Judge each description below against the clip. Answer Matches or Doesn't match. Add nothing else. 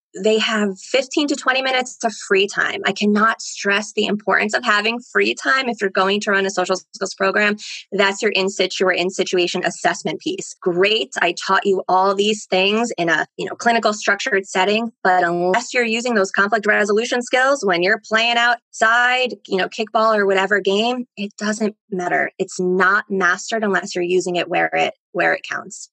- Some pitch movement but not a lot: Matches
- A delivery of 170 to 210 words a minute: Matches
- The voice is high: Matches